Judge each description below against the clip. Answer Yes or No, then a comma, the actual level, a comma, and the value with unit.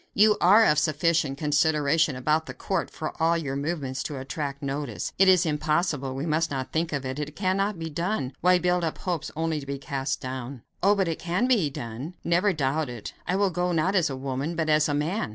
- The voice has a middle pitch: Yes, medium, 155 Hz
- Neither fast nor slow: No, fast, 225 wpm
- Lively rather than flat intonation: No, average, 4.0 semitones